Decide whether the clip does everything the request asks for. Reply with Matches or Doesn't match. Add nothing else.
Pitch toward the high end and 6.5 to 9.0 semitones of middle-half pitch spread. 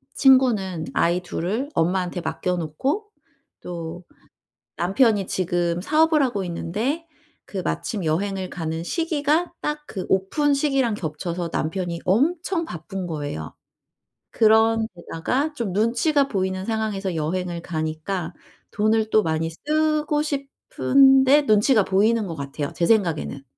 Matches